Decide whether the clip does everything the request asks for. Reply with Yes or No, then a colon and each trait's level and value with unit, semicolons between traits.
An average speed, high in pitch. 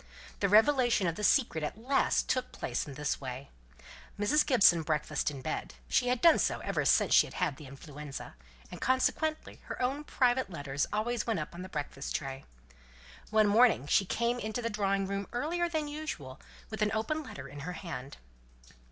Yes: average, 185 wpm; high, 205 Hz